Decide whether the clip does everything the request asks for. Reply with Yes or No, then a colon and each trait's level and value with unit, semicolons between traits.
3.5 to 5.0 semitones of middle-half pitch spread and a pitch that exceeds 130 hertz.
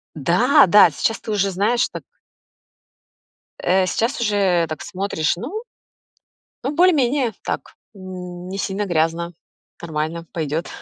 Yes: average, 4.7 semitones; high, 190 Hz